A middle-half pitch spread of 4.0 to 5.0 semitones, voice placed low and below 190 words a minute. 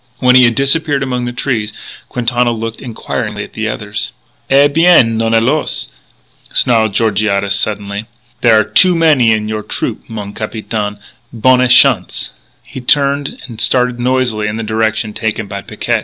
No: average, 3.0 semitones; low, 115 Hz; average, 155 wpm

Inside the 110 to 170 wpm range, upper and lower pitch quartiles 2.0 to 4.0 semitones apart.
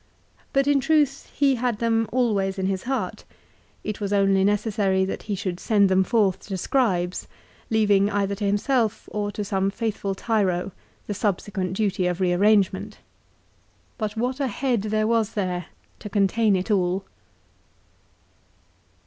Yes: average, 150 wpm; average, 2.8 semitones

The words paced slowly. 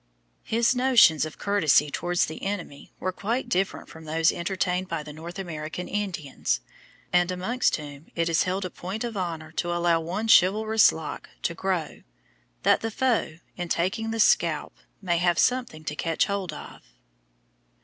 No: average, 165 wpm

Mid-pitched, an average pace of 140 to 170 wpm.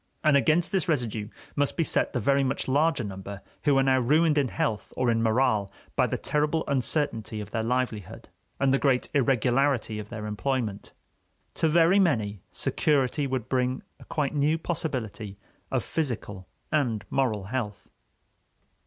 No: low, 130 Hz; average, 160 wpm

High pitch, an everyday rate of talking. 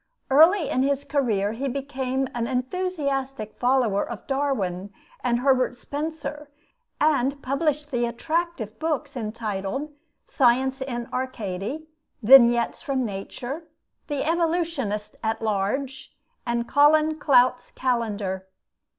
No: very high, 265 Hz; slow, 105 wpm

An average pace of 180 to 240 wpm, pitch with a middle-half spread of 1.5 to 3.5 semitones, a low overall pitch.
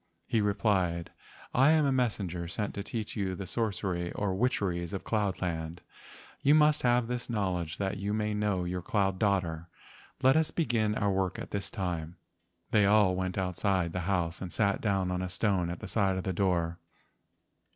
Yes: average, 185 wpm; average, 3.0 semitones; very low, 95 Hz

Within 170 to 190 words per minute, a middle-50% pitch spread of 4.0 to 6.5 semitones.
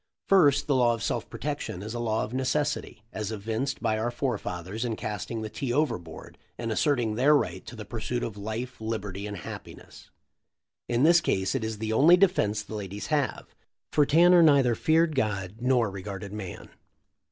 Yes: average, 180 wpm; average, 4.7 semitones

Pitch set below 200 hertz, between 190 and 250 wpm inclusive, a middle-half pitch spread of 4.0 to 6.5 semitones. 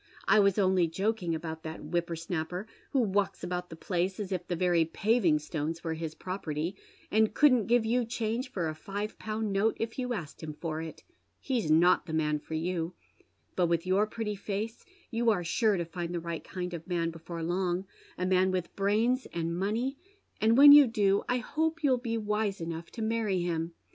Yes: medium, 185 Hz; average, 200 wpm; average, 4.8 semitones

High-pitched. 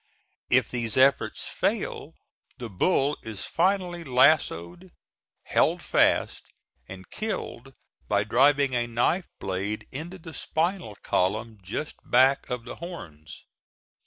No: low, 125 Hz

